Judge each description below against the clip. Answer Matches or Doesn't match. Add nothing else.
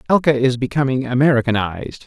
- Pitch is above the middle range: Doesn't match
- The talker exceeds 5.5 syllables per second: Matches